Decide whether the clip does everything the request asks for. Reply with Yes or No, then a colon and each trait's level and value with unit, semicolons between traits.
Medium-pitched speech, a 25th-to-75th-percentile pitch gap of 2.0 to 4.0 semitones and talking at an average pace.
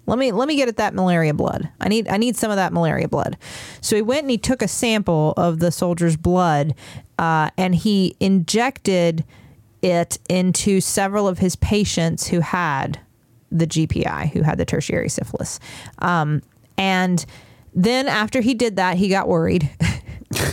No: medium, 180 Hz; average, 4.6 semitones; average, 170 wpm